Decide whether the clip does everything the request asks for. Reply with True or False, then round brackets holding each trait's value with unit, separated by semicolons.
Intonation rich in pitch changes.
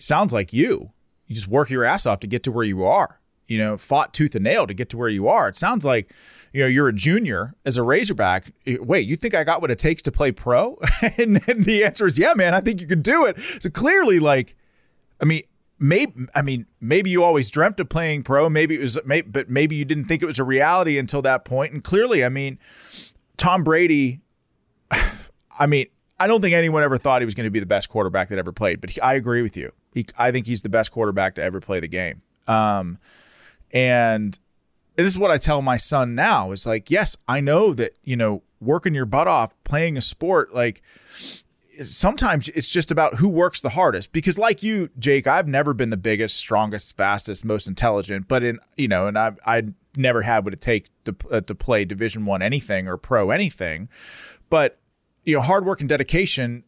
True (5.9 semitones)